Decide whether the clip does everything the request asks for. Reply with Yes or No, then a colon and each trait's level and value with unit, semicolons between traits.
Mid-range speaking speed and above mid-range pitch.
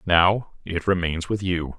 No: average, 170 wpm; very low, 90 Hz